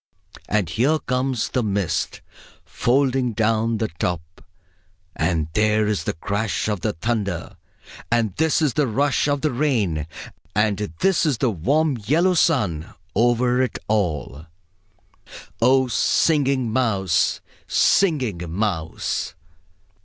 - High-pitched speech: No, low, 115 Hz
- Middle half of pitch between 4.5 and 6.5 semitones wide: Yes, average, 5.2 semitones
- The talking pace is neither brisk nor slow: No, slow, 120 wpm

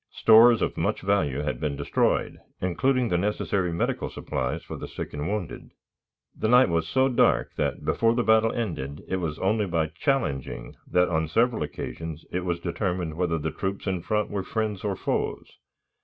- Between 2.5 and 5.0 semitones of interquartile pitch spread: No, wide, 5.4 semitones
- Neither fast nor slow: Yes, average, 180 wpm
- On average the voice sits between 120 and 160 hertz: No, very low, 90 Hz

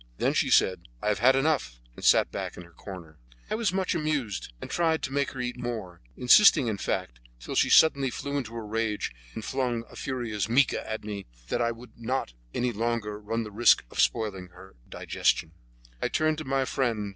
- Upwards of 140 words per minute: Yes, fast, 205 wpm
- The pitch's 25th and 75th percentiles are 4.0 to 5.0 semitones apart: Yes, average, 4.4 semitones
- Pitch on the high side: No, low, 115 Hz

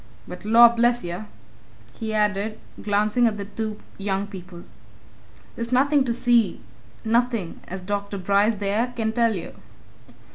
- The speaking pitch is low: No, high, 215 Hz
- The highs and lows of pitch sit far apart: No, average, 2.7 semitones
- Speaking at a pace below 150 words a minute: Yes, average, 140 wpm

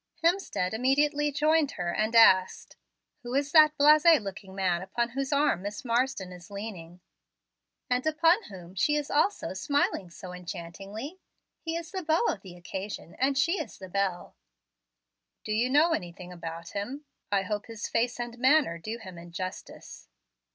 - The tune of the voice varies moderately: No, wide, 7.8 semitones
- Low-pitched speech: No, high, 225 Hz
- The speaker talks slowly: No, average, 160 wpm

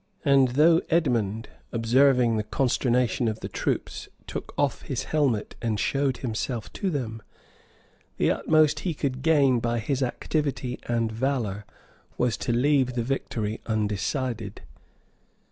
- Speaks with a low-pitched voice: Yes, low, 125 Hz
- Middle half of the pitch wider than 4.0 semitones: No, average, 3.6 semitones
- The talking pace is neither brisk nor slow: No, slow, 130 wpm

